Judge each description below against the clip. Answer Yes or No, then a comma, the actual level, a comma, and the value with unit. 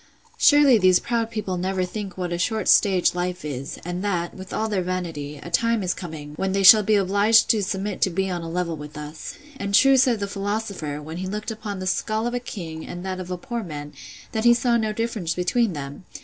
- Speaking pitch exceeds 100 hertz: Yes, high, 190 Hz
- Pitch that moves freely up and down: No, average, 3.8 semitones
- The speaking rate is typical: No, fast, 235 wpm